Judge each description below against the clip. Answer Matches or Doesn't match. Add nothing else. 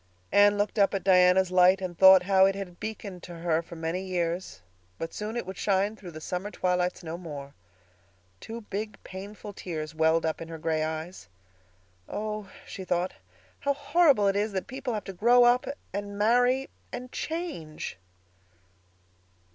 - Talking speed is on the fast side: Doesn't match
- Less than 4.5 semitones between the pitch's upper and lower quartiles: Matches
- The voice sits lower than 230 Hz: Matches